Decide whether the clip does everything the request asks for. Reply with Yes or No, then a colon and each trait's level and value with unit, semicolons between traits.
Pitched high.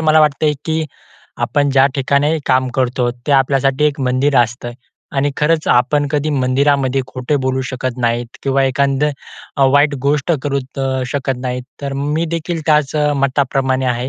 No: low, 135 Hz